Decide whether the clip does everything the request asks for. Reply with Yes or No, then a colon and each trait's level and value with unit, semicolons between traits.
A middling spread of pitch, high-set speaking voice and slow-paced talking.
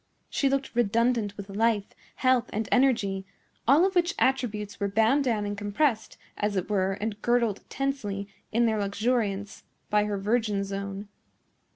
No: average, 3.4 semitones; high, 215 Hz; average, 155 wpm